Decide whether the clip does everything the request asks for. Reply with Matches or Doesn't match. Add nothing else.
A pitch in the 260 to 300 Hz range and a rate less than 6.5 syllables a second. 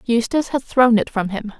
Doesn't match